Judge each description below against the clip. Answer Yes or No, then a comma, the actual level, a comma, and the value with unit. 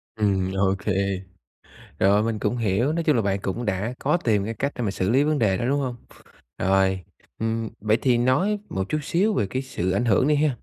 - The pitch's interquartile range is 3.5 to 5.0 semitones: No, wide, 5.6 semitones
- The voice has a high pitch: No, low, 115 Hz